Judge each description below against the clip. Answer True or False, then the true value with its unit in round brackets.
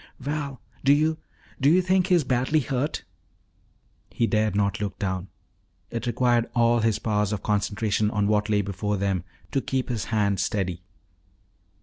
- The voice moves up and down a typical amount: True (4.5 semitones)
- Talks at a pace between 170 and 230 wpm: False (160 wpm)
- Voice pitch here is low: True (110 Hz)